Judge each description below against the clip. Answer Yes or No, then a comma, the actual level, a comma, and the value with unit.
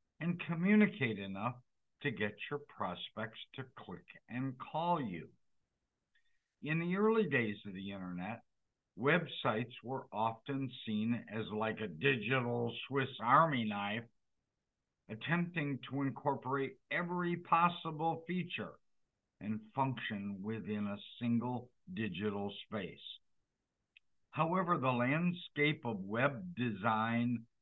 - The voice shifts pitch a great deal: Yes, wide, 6.3 semitones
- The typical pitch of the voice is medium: No, low, 125 Hz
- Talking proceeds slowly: Yes, slow, 105 wpm